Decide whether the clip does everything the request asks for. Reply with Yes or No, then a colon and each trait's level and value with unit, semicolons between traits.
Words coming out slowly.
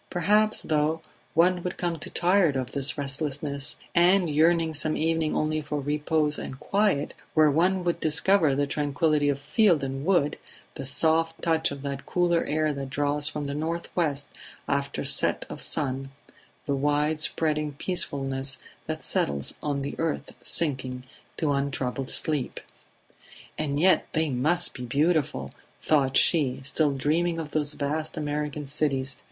No: average, 150 wpm